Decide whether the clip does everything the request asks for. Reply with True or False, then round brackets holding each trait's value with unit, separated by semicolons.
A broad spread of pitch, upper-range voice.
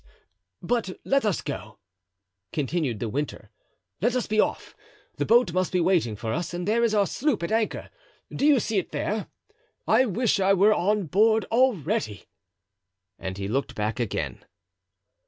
True (7.1 semitones; 195 Hz)